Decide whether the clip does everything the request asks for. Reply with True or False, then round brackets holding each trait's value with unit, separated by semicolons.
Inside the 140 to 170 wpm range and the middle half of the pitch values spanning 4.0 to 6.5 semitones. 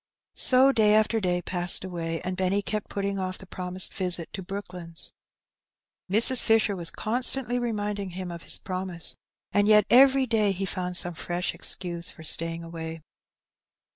False (160 wpm; 3.3 semitones)